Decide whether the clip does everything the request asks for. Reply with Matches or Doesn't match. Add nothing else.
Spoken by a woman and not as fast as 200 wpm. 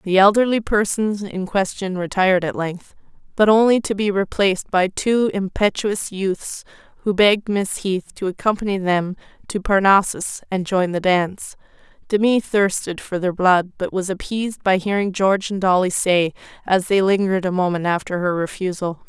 Matches